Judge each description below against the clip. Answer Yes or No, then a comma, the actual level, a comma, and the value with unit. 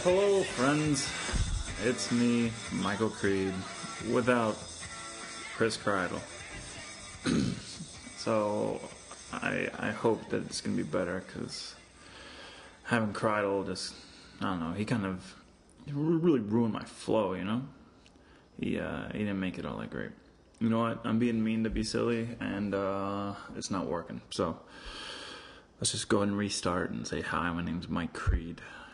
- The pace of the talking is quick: No, average, 150 wpm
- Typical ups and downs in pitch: Yes, average, 3.7 semitones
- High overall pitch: No, low, 105 Hz